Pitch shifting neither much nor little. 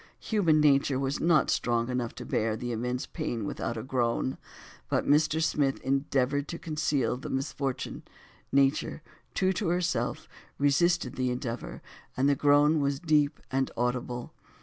Yes: average, 3.4 semitones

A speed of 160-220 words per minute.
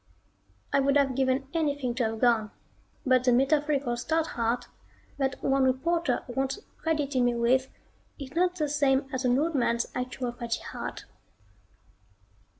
No: average, 150 wpm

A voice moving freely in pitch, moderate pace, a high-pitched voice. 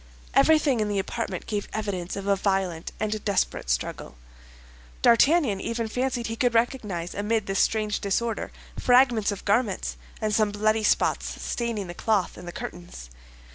No: average, 3.1 semitones; average, 155 wpm; high, 210 Hz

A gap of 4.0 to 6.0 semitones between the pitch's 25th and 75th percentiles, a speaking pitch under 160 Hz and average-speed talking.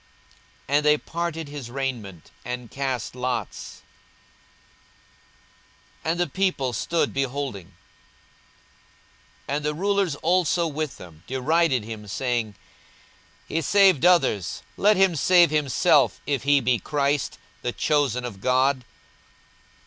No: average, 4.8 semitones; medium, 140 Hz; slow, 115 wpm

